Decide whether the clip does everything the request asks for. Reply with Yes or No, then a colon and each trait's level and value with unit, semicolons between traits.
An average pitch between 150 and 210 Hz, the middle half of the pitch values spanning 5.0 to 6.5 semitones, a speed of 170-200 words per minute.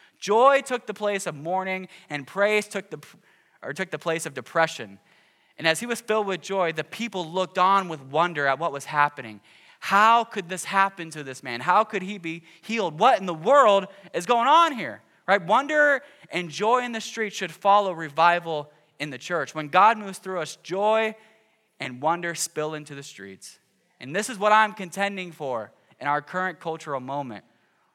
Yes: medium, 185 Hz; average, 5.3 semitones; average, 195 wpm